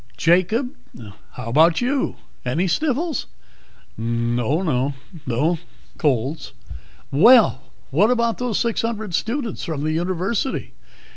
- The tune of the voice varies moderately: No, wide, 9.0 semitones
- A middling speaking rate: No, slow, 110 wpm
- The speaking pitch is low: No, medium, 175 Hz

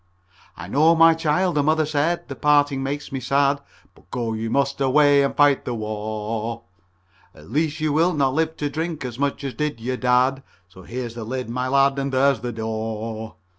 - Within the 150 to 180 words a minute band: No, average, 200 wpm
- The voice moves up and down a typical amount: Yes, average, 4.1 semitones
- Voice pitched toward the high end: No, low, 135 Hz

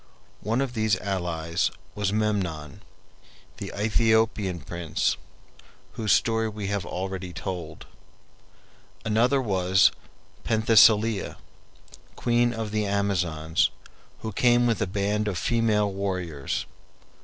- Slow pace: Yes, slow, 105 wpm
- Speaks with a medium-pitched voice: No, low, 100 Hz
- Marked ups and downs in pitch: No, average, 3.3 semitones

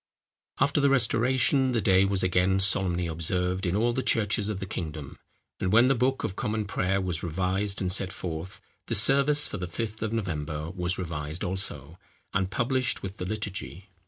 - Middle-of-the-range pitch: No, very low, 95 Hz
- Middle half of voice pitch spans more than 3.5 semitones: Yes, average, 3.9 semitones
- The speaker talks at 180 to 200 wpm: Yes, average, 185 wpm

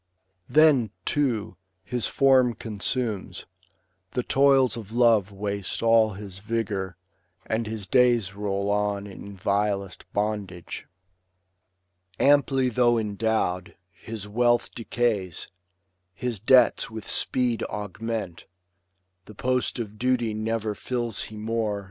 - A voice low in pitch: Yes, low, 110 Hz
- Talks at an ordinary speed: No, slow, 110 wpm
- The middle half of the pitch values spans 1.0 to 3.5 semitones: Yes, average, 3.0 semitones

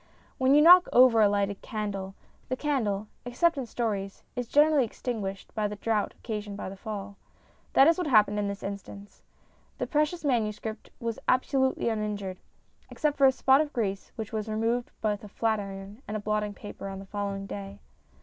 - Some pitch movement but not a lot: Yes, average, 4.0 semitones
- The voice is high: Yes, high, 215 Hz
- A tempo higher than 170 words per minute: Yes, average, 180 wpm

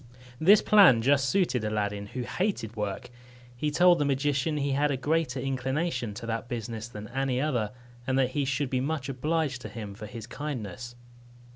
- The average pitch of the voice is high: No, low, 130 Hz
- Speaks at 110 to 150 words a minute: No, average, 185 wpm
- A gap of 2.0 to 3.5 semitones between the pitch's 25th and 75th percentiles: No, average, 4.2 semitones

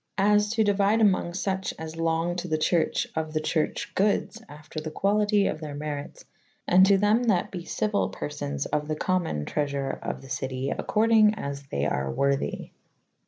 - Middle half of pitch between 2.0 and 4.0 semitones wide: No, wide, 5.6 semitones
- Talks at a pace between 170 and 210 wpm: Yes, average, 175 wpm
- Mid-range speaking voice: Yes, medium, 165 Hz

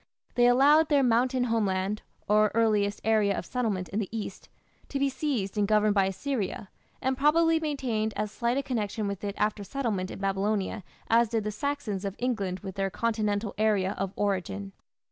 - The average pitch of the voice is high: Yes, high, 215 Hz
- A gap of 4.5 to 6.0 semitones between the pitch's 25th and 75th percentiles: No, average, 3.7 semitones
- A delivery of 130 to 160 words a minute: No, average, 180 wpm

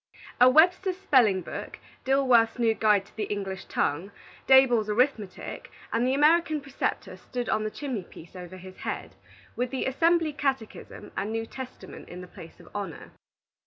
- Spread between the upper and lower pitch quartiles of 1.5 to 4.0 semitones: No, average, 5.1 semitones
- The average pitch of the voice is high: Yes, high, 240 Hz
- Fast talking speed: No, average, 160 wpm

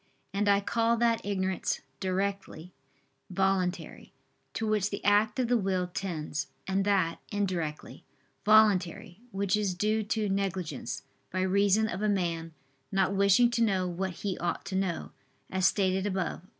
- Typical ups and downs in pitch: No, narrow, 2.0 semitones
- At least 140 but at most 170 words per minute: Yes, average, 150 wpm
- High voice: Yes, high, 195 Hz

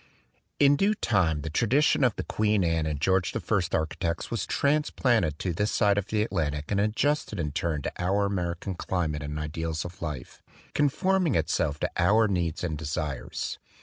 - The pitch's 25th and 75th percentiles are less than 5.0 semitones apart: No, wide, 5.6 semitones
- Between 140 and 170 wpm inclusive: No, average, 180 wpm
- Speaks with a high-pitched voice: No, very low, 90 Hz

